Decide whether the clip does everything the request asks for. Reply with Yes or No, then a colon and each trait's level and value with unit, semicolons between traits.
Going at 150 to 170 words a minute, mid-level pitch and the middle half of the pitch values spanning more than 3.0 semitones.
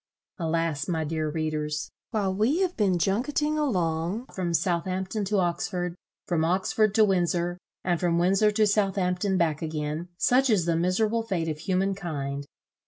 Yes: average, 155 wpm; medium, 180 Hz; average, 3.8 semitones